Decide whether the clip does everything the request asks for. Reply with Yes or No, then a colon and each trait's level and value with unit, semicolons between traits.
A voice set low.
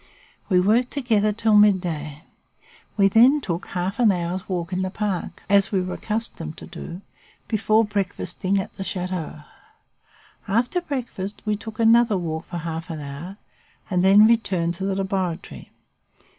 No: high, 195 Hz